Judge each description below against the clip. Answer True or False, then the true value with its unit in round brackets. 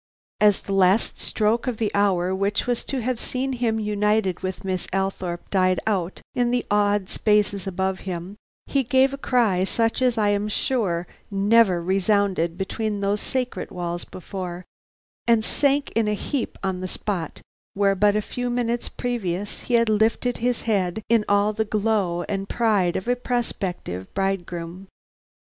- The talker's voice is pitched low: False (205 Hz)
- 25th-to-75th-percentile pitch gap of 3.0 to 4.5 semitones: True (3.4 semitones)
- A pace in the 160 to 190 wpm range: True (165 wpm)